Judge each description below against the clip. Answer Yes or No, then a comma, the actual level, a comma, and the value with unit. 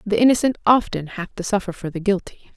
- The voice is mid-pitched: No, high, 200 Hz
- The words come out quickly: Yes, fast, 210 wpm